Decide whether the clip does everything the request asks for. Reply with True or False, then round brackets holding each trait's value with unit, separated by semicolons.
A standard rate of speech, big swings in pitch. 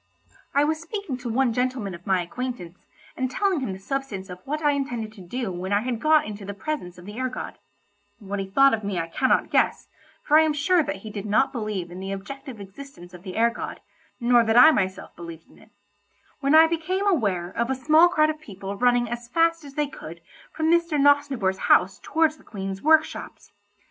False (220 wpm; 7.2 semitones)